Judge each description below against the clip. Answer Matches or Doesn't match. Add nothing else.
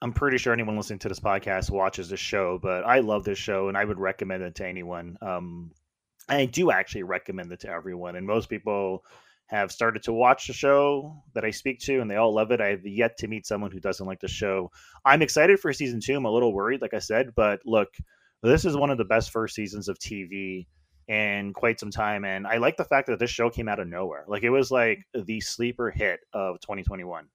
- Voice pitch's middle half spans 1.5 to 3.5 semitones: Doesn't match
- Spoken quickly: Matches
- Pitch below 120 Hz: Matches